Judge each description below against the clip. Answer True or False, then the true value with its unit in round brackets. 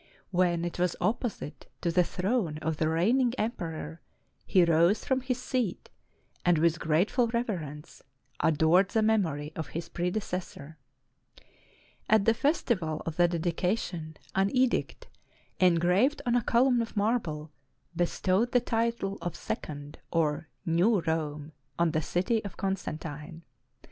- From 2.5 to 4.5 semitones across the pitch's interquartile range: False (5.5 semitones)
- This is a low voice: False (175 Hz)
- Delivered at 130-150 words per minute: True (140 wpm)